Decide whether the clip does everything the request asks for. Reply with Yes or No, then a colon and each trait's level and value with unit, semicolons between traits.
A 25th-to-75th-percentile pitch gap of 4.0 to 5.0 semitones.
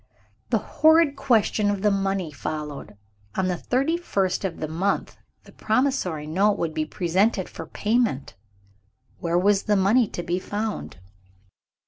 Yes: average, 4.4 semitones